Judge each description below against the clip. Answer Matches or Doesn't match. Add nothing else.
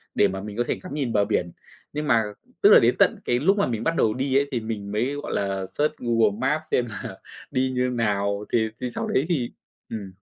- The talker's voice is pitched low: Matches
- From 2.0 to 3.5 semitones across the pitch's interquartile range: Doesn't match